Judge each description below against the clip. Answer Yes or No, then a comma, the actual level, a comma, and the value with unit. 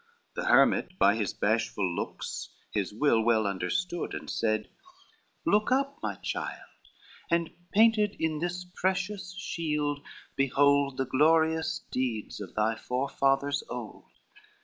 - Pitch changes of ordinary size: No, wide, 7.6 semitones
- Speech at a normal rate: No, slow, 125 wpm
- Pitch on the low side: No, medium, 145 Hz